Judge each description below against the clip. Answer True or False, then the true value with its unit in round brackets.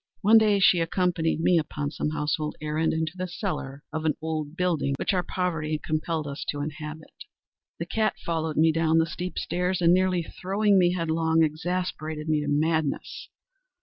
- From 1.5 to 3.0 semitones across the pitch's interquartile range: True (2.7 semitones)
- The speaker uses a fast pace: False (175 wpm)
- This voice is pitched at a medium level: True (160 Hz)